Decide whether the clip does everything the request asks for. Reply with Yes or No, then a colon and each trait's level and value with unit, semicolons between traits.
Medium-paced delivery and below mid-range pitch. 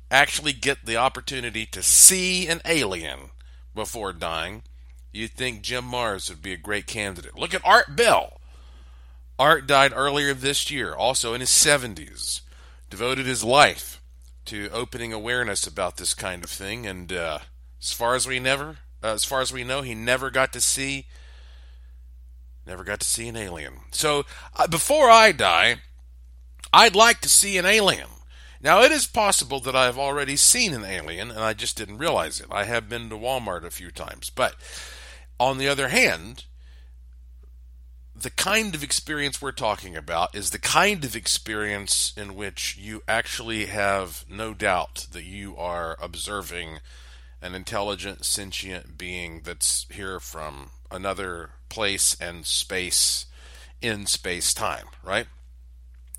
Yes: average, 155 wpm; very low, 95 Hz